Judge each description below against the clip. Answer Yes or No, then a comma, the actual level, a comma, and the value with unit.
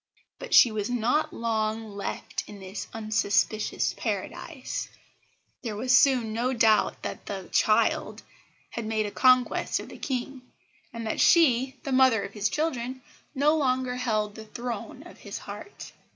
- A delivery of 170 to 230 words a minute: No, average, 150 wpm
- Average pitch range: Yes, average, 3.0 semitones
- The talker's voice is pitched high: Yes, high, 235 Hz